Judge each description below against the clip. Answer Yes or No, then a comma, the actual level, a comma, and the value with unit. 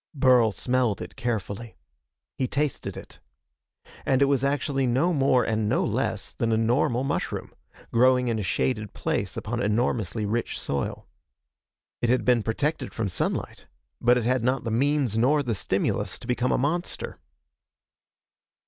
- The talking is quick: No, average, 155 wpm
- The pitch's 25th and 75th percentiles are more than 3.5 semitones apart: No, average, 3.0 semitones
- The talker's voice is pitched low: Yes, low, 120 Hz